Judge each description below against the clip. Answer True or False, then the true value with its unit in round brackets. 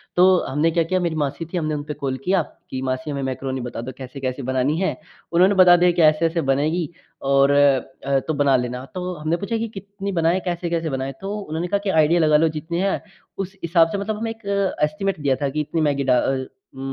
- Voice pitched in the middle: True (155 Hz)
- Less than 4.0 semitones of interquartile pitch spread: False (4.6 semitones)